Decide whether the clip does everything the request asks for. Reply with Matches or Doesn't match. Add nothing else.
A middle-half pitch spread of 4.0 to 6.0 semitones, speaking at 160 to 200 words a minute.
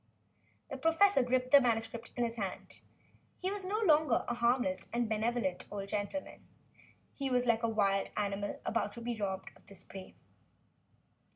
Matches